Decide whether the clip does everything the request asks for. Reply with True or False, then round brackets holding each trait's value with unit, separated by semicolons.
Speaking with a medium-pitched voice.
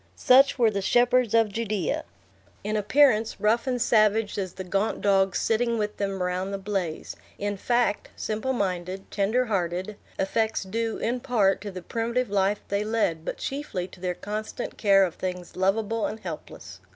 False (210 Hz)